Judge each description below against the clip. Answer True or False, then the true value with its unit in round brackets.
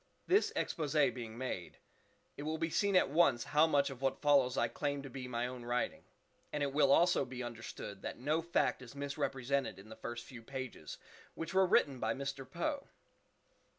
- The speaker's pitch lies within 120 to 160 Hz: True (135 Hz)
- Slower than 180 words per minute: False (185 wpm)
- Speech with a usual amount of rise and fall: True (3.5 semitones)